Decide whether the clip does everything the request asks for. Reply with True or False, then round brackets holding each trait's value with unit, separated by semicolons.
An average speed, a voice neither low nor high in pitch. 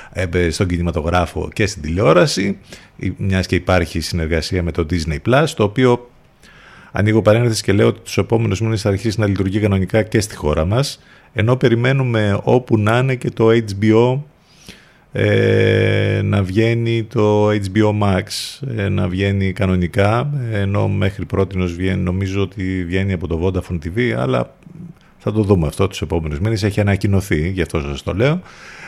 False (160 wpm; 100 Hz)